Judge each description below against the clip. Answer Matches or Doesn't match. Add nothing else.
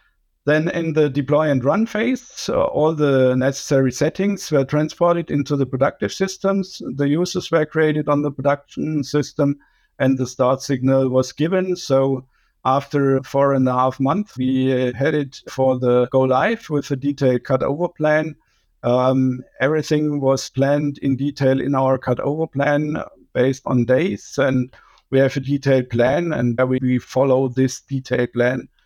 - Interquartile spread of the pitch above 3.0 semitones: Doesn't match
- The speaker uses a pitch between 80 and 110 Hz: Doesn't match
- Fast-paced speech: Doesn't match